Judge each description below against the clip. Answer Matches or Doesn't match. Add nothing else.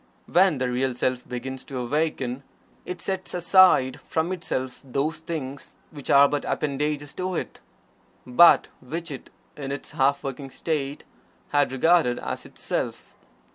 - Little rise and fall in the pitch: Doesn't match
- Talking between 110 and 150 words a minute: Matches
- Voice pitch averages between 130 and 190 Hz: Matches